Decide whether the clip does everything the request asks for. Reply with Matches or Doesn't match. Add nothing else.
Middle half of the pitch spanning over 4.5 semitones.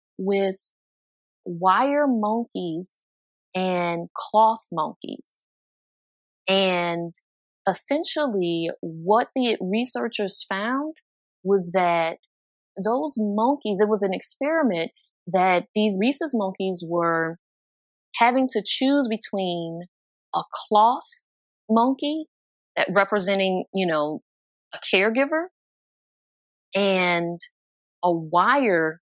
Matches